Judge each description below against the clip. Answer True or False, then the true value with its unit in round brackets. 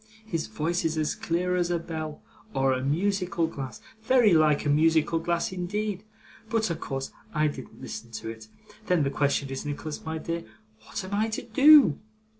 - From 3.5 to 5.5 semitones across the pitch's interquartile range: True (4.0 semitones)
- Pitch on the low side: False (165 Hz)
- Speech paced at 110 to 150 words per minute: False (185 wpm)